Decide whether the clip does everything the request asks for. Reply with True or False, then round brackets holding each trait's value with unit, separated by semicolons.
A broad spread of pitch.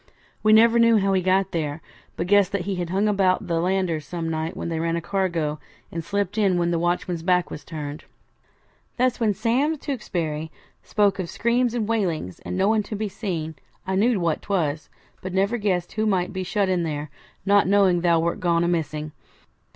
False (3.5 semitones)